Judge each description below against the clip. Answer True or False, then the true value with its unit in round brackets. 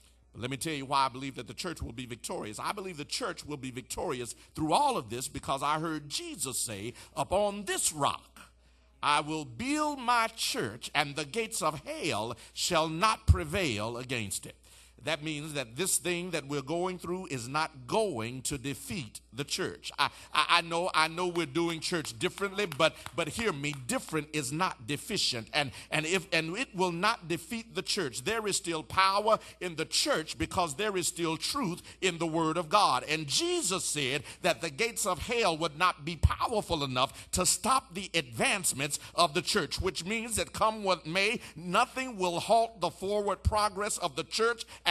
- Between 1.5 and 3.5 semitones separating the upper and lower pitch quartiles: False (4.8 semitones)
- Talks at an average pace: True (190 wpm)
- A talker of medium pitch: True (170 Hz)